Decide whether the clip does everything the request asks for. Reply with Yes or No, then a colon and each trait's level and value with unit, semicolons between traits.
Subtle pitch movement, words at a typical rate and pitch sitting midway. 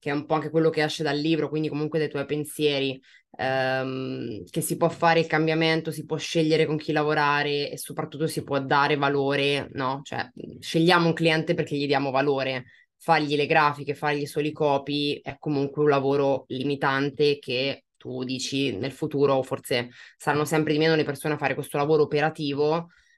No: narrow, 2.1 semitones; fast, 185 wpm; medium, 145 Hz